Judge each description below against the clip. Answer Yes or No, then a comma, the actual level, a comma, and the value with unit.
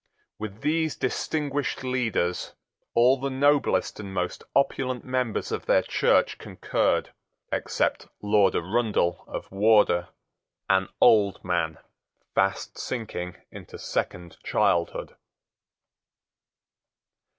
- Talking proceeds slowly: Yes, slow, 95 wpm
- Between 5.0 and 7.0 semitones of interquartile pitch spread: Yes, wide, 5.5 semitones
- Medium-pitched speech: No, low, 110 Hz